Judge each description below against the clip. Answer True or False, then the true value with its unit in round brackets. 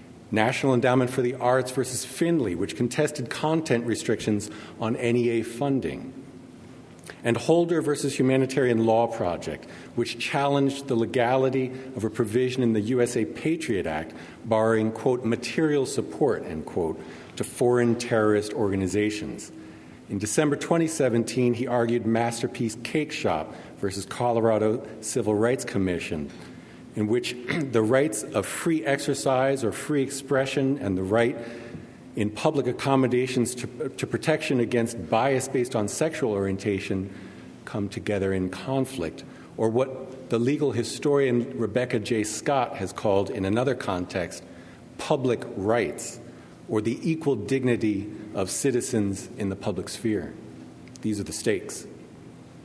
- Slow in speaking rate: True (130 wpm)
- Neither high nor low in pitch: False (120 Hz)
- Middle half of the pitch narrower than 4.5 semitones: True (3.8 semitones)